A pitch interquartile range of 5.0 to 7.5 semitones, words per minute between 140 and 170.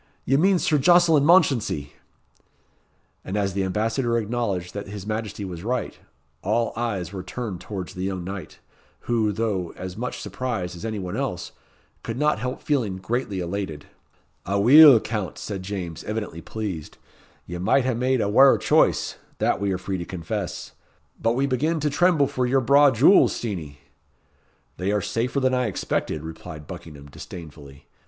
Yes: wide, 5.5 semitones; average, 160 wpm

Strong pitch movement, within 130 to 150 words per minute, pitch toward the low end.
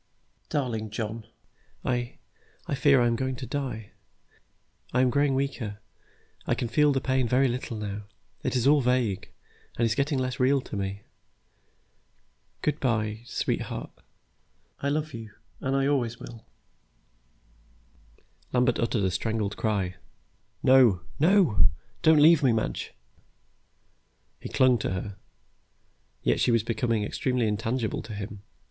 No: average, 3.8 semitones; average, 140 wpm; low, 120 Hz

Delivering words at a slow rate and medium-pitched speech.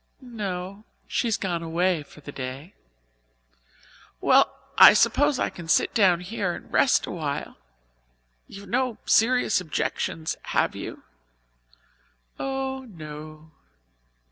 Yes: slow, 115 wpm; medium, 180 Hz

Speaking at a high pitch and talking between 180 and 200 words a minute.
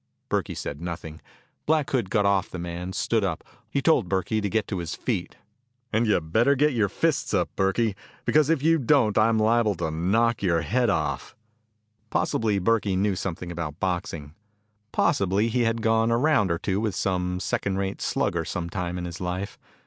No: low, 100 Hz; average, 185 wpm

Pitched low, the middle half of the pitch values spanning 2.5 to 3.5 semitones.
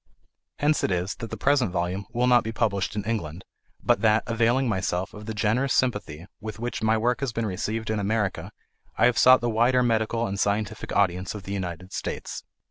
Yes: low, 110 Hz; average, 3.1 semitones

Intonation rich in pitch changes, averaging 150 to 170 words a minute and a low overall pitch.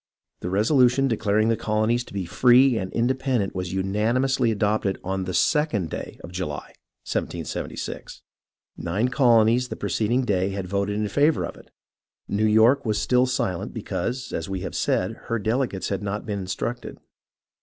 No: average, 4.2 semitones; average, 160 wpm; low, 110 Hz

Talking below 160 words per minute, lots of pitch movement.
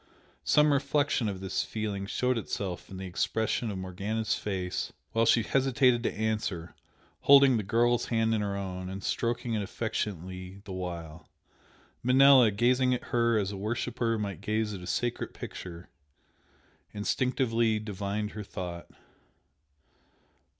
No: average, 140 wpm; average, 3.8 semitones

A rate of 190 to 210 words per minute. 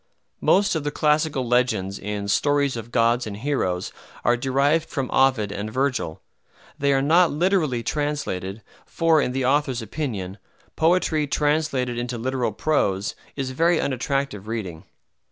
No: average, 140 wpm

